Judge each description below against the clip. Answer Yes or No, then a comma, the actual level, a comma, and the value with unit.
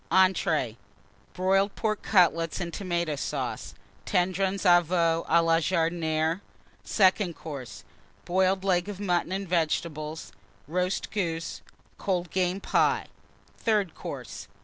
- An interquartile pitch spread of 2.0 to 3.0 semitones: Yes, narrow, 2.4 semitones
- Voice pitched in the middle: Yes, medium, 175 Hz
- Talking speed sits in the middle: No, slow, 115 wpm